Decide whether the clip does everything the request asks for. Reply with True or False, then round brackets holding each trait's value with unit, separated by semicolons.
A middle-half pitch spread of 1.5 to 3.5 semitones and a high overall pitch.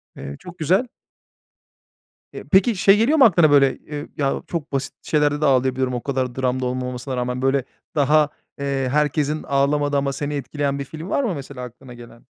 False (2.7 semitones; 140 Hz)